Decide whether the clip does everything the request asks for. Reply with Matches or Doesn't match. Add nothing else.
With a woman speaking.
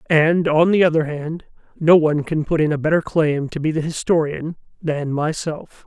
Doesn't match